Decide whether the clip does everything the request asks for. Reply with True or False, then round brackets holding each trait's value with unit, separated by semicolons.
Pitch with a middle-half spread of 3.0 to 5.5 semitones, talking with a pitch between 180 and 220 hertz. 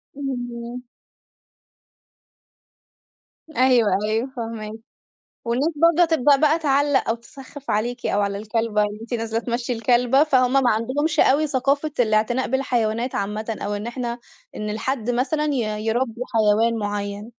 False (3.5 semitones; 240 Hz)